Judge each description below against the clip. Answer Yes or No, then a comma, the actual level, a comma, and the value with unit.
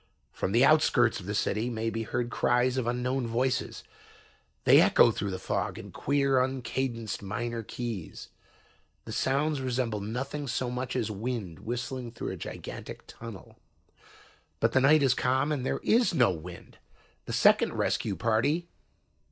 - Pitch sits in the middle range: No, low, 120 Hz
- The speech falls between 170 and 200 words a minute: No, average, 155 wpm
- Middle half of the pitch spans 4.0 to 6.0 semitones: No, average, 2.9 semitones